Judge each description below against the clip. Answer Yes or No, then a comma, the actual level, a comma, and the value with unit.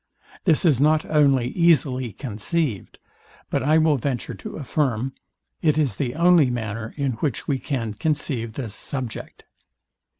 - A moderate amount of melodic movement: Yes, average, 4.6 semitones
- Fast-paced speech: No, average, 140 wpm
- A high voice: No, low, 135 Hz